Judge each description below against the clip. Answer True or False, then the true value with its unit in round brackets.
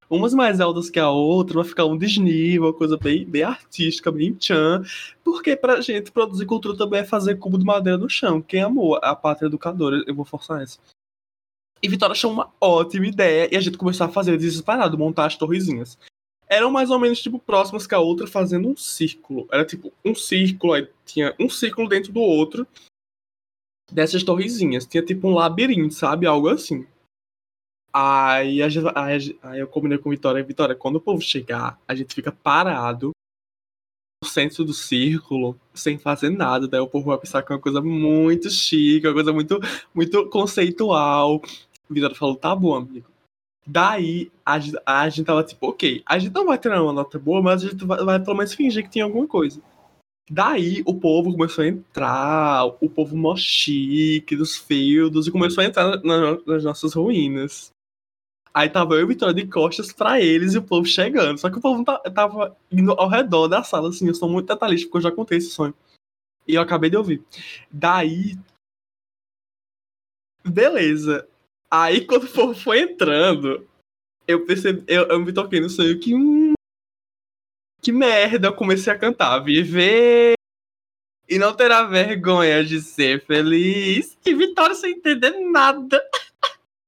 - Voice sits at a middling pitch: True (175 Hz)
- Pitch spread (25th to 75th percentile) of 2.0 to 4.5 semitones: False (5.5 semitones)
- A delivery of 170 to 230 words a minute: True (175 wpm)